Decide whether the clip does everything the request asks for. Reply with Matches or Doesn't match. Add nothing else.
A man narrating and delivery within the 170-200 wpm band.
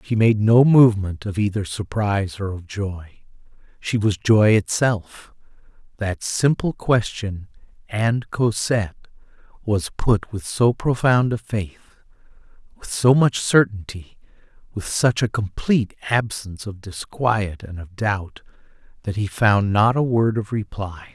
Doesn't match